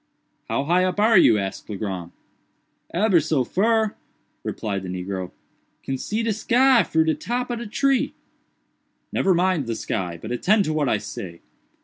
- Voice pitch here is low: No, medium, 160 Hz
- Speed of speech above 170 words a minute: No, average, 165 wpm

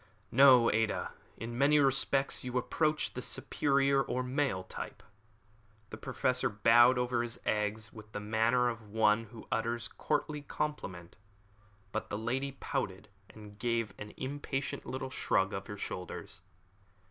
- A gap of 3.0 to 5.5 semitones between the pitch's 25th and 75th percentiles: Yes, average, 4.1 semitones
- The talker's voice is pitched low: Yes, low, 120 Hz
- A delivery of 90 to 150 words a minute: Yes, average, 145 wpm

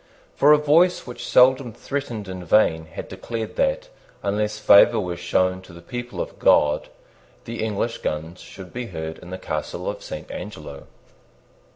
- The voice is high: No, low, 105 Hz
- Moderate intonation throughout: No, wide, 5.8 semitones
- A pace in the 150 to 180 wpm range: Yes, average, 165 wpm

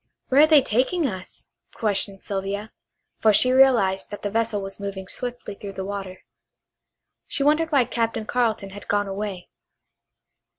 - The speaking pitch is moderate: No, high, 210 Hz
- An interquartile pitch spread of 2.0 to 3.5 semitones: No, average, 4.2 semitones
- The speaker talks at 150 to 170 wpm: Yes, average, 155 wpm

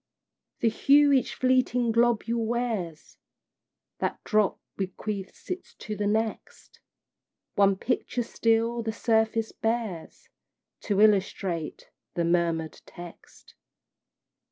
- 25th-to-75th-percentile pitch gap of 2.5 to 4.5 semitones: Yes, average, 3.5 semitones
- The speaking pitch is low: No, high, 220 Hz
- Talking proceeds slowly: Yes, slow, 100 wpm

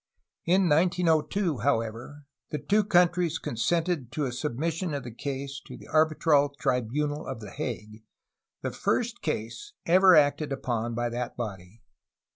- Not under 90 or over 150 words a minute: Yes, average, 145 wpm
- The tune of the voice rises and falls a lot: Yes, wide, 5.8 semitones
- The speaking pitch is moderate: Yes, medium, 145 Hz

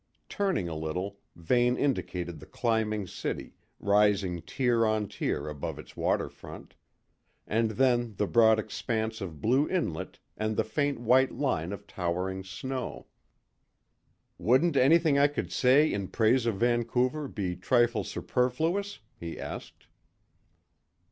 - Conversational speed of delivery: No, slow, 130 wpm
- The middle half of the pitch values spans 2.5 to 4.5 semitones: No, average, 5.2 semitones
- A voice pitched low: Yes, low, 115 Hz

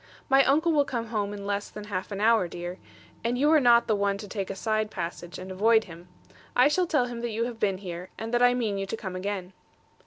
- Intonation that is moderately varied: Yes, average, 3.8 semitones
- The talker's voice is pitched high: Yes, high, 215 Hz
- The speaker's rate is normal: No, fast, 255 wpm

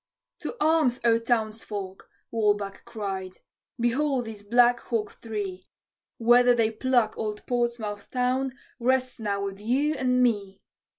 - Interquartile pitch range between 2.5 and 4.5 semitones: Yes, average, 3.2 semitones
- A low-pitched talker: No, high, 230 Hz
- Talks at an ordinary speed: No, slow, 125 wpm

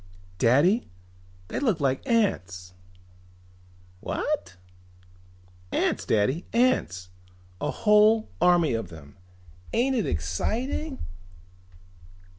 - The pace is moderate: No, slow, 80 wpm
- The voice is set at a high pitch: No, medium, 165 Hz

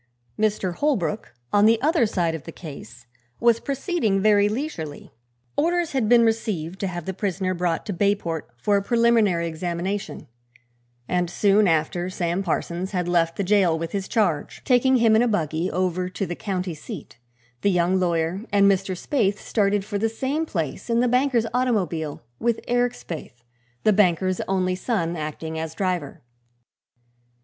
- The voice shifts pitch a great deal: No, average, 4.6 semitones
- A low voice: No, high, 190 Hz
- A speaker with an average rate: Yes, average, 165 wpm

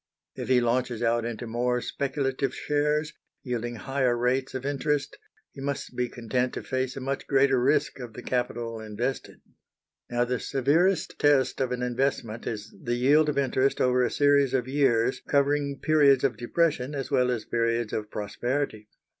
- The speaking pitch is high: No, low, 130 Hz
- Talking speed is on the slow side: No, average, 170 wpm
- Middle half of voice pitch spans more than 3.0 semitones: No, narrow, 2.6 semitones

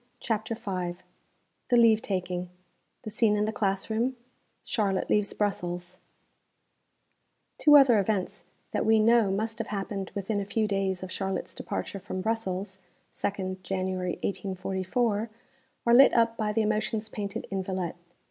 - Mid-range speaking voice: No, high, 205 Hz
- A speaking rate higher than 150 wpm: No, average, 145 wpm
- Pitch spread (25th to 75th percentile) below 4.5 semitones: Yes, average, 2.9 semitones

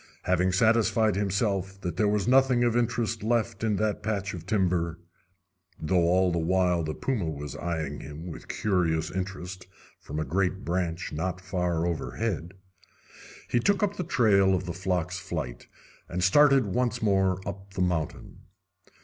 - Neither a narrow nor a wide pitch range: Yes, average, 3.8 semitones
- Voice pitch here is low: Yes, very low, 95 Hz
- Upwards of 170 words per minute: No, average, 160 wpm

